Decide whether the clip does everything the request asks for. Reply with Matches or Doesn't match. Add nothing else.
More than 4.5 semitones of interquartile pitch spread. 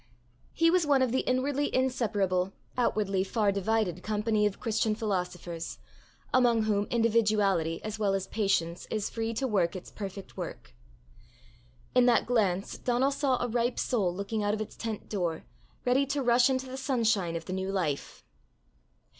Doesn't match